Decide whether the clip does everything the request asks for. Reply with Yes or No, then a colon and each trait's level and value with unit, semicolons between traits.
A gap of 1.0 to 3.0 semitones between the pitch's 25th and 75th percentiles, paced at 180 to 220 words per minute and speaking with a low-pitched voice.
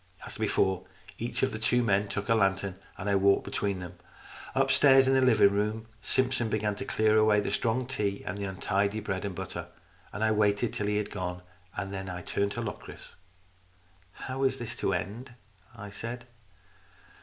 Yes: narrow, 2.6 semitones; average, 190 wpm; low, 105 Hz